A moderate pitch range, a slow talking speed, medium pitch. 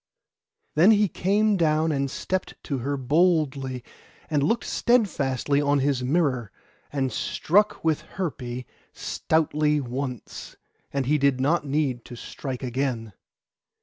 Yes: average, 3.6 semitones; slow, 125 wpm; medium, 145 Hz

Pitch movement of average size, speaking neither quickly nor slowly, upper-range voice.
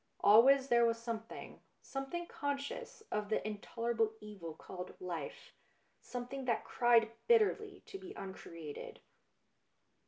No: average, 4.7 semitones; slow, 120 wpm; high, 230 Hz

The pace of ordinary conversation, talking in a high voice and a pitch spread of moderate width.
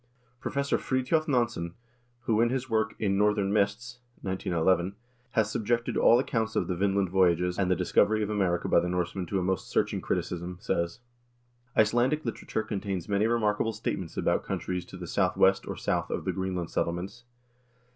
No: average, 170 wpm; low, 100 Hz; average, 3.8 semitones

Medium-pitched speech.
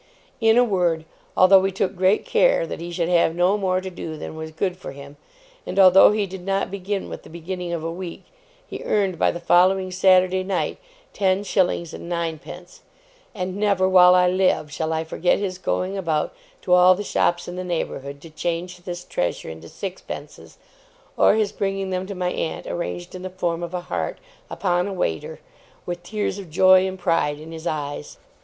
Yes: medium, 180 Hz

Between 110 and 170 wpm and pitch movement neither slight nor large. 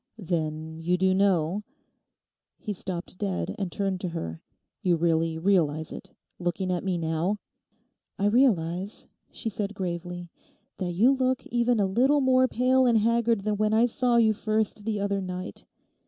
Yes: average, 160 wpm; average, 4.5 semitones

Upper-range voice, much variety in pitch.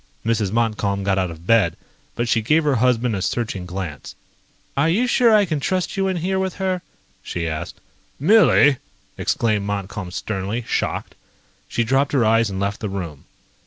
No: low, 115 Hz; wide, 7.4 semitones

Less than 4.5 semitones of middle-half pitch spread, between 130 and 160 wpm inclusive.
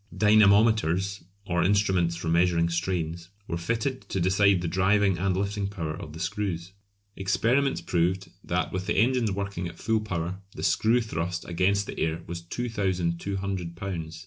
Yes: average, 3.1 semitones; average, 155 wpm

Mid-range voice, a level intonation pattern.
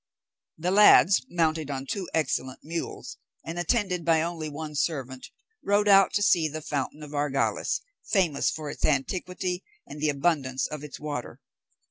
No: medium, 155 Hz; average, 3.7 semitones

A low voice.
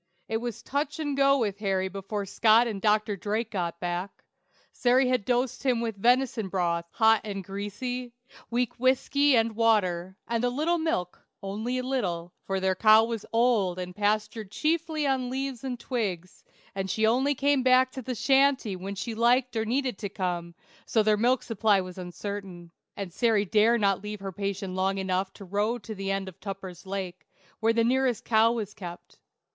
No: high, 215 Hz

